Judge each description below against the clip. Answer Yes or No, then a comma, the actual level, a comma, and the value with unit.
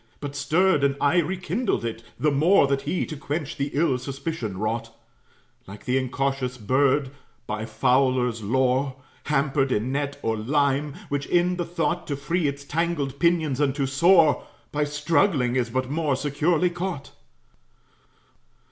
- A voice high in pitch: No, medium, 140 Hz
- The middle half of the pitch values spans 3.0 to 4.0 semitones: Yes, average, 3.5 semitones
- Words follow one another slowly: No, average, 150 wpm